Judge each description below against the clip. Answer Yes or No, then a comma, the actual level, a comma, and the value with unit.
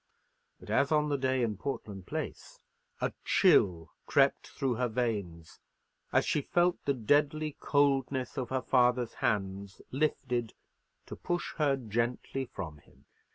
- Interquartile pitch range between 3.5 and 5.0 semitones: Yes, average, 4.7 semitones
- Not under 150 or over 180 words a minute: No, average, 140 wpm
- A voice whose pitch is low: Yes, low, 125 Hz